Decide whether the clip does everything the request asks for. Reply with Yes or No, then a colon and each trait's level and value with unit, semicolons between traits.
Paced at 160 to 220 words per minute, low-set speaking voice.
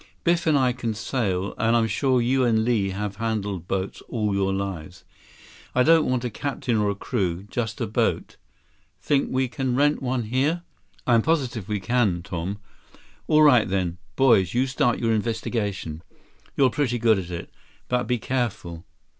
Yes: average, 170 wpm; low, 115 Hz